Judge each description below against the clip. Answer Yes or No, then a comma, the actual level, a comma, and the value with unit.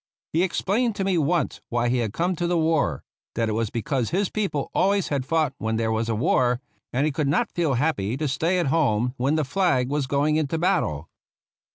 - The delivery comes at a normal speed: No, fast, 225 wpm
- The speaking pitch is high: No, medium, 145 Hz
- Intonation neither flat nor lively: No, wide, 6.0 semitones